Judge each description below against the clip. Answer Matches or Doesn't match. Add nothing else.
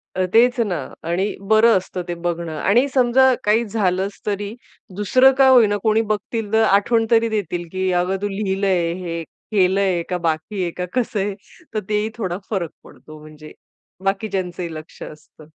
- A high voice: Matches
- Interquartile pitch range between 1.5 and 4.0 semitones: Matches